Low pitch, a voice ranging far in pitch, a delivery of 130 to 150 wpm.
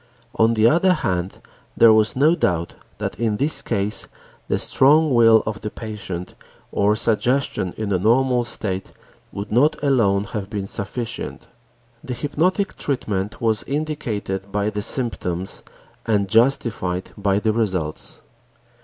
No: low, 110 Hz; average, 4.0 semitones; slow, 135 wpm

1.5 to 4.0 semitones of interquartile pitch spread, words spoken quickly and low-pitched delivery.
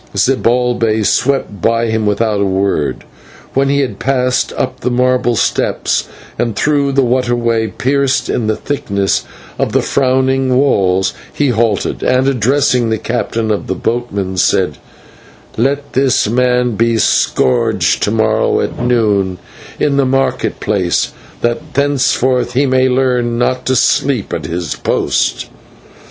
No: average, 3.3 semitones; average, 145 wpm; low, 120 Hz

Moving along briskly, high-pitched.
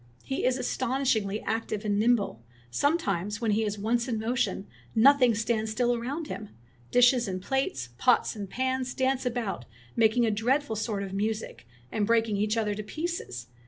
No: average, 170 wpm; high, 225 Hz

